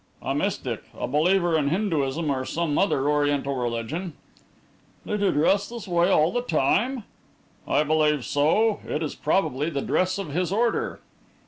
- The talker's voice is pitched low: No, medium, 160 Hz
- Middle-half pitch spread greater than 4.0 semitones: Yes, average, 5.1 semitones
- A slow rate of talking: No, average, 155 wpm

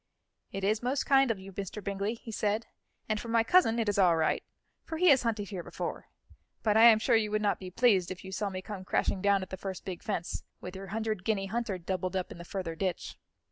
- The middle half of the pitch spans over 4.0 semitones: No, average, 3.0 semitones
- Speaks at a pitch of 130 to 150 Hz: No, high, 200 Hz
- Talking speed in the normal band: No, fast, 250 wpm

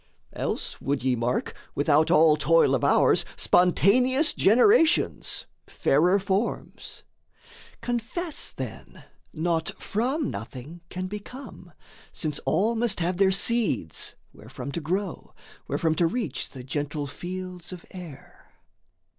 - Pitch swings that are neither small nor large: No, wide, 6.5 semitones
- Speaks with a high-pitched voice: No, medium, 180 Hz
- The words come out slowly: Yes, slow, 115 wpm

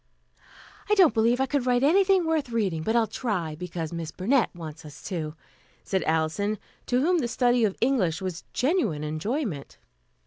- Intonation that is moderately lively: No, wide, 8.2 semitones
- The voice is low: No, high, 220 Hz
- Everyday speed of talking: Yes, average, 170 wpm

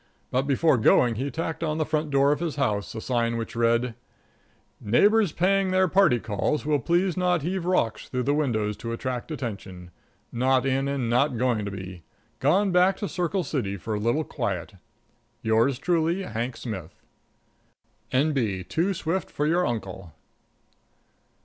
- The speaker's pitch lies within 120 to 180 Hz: Yes, low, 135 Hz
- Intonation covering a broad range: Yes, wide, 6.3 semitones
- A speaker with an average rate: Yes, average, 160 wpm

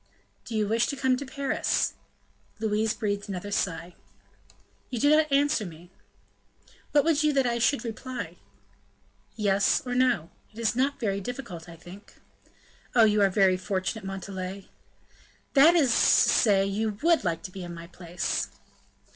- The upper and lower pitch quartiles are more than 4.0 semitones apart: Yes, average, 5.2 semitones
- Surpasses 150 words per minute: Yes, average, 160 wpm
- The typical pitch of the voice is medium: No, high, 215 Hz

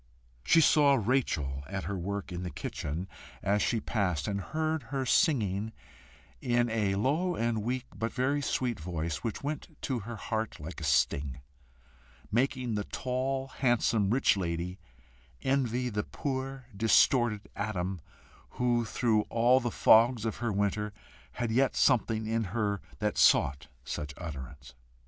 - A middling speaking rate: Yes, average, 145 wpm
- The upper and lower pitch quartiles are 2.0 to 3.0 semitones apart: No, average, 4.9 semitones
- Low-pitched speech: Yes, low, 110 Hz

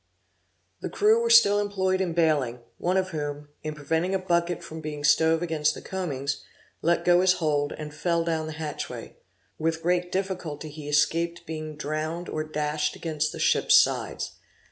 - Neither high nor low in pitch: Yes, medium, 160 Hz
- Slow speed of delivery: No, average, 170 wpm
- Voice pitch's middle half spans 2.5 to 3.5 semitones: Yes, average, 2.8 semitones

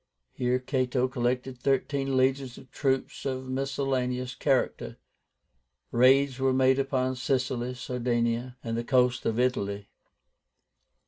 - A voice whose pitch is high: No, low, 130 Hz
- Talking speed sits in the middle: No, slow, 115 wpm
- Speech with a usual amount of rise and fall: No, narrow, 1.3 semitones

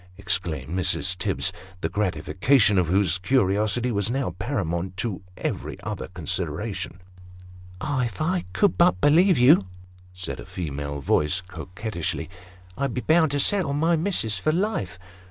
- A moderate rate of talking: Yes, average, 155 wpm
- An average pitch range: No, wide, 7.0 semitones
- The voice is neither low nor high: No, very low, 95 Hz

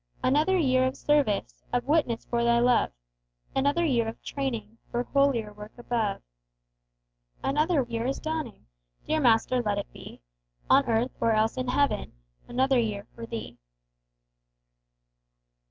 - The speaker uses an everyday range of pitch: Yes, average, 3.6 semitones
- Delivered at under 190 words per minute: Yes, average, 140 wpm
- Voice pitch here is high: Yes, high, 245 Hz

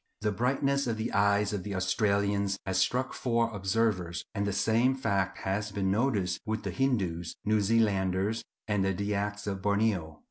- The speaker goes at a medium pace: Yes, average, 165 wpm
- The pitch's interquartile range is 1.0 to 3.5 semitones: Yes, narrow, 2.6 semitones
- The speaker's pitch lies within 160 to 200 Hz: No, low, 100 Hz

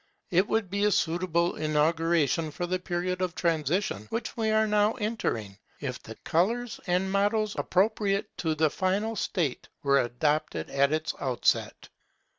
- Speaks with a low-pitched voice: No, medium, 175 Hz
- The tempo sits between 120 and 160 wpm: Yes, average, 150 wpm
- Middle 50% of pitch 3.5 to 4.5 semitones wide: No, average, 5.0 semitones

